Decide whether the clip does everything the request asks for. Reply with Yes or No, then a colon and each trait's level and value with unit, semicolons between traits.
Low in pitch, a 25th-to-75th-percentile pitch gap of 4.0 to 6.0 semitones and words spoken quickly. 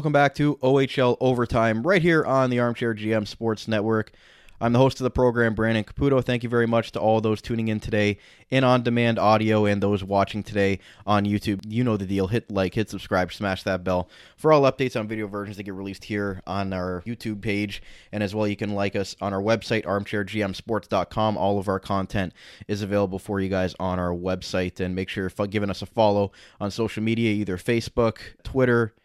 No: low, 105 Hz; average, 2.9 semitones; fast, 215 wpm